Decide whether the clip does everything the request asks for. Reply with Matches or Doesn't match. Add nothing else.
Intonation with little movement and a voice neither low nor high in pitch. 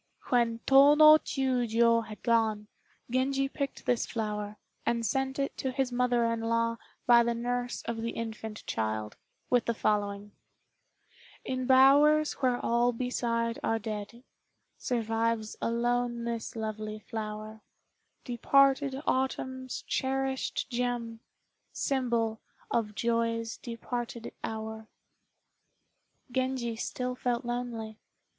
Doesn't match